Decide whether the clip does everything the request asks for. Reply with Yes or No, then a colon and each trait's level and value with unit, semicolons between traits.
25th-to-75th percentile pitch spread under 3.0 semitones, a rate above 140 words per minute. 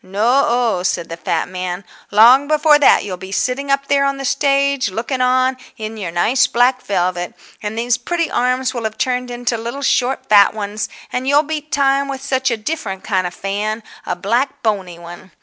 No: average, 5.3 semitones; average, 195 wpm